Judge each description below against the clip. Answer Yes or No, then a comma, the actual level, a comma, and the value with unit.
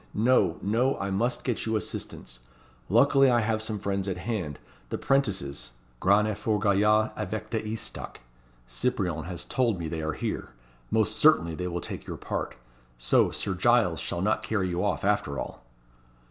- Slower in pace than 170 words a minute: No, average, 175 wpm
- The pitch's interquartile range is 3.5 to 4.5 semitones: Yes, average, 4.0 semitones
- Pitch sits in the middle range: No, low, 100 Hz